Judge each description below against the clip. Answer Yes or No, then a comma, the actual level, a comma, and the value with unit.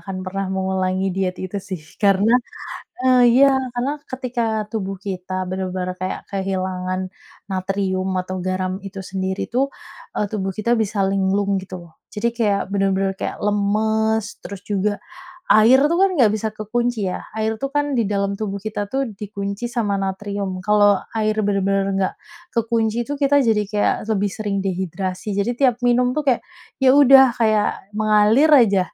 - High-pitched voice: Yes, high, 205 Hz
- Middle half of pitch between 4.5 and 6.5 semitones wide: No, average, 3.2 semitones